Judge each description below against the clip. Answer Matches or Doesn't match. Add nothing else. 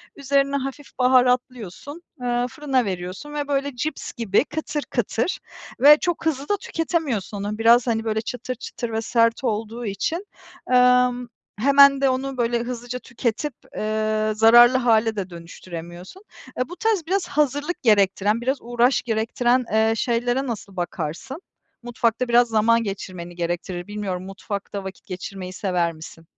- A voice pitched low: Doesn't match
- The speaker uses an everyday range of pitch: Matches